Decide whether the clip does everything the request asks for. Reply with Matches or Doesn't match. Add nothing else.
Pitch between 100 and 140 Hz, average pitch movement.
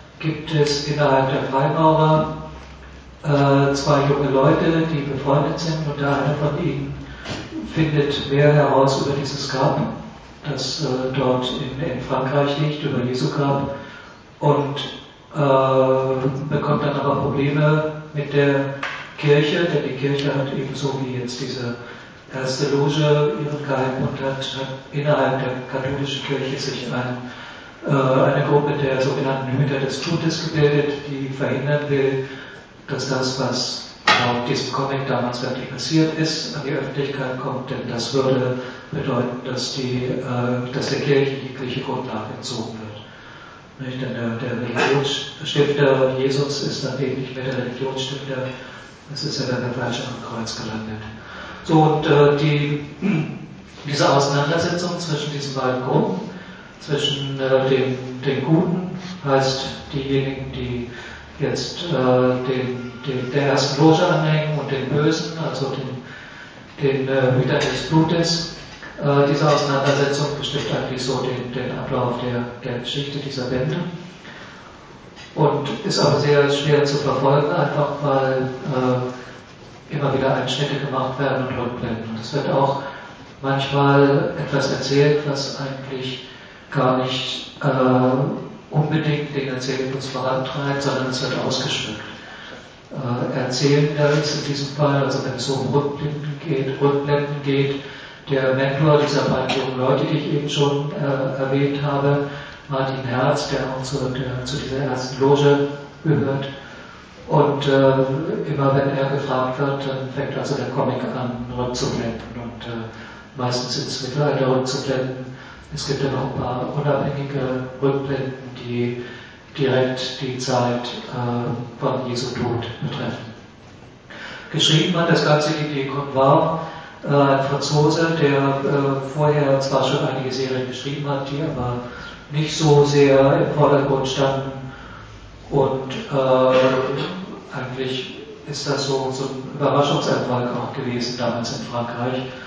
Doesn't match